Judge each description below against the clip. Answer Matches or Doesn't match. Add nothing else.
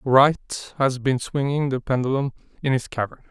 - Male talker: Matches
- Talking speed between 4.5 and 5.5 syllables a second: Matches